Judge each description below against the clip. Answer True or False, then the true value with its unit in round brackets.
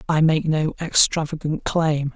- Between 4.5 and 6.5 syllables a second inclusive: False (4.1 syllables/s)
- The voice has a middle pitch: True (155 Hz)